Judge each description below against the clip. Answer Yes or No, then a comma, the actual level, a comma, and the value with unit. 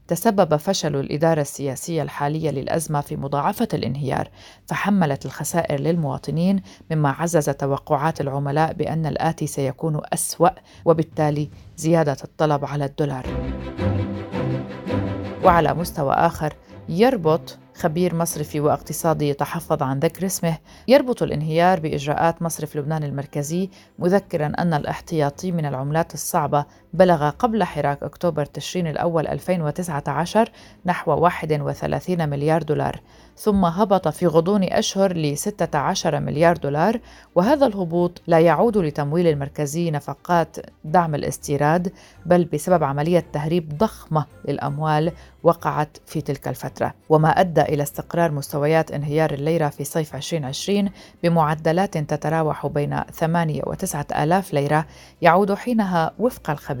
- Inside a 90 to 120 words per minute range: Yes, average, 115 wpm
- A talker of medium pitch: Yes, medium, 160 Hz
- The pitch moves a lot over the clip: No, average, 3.0 semitones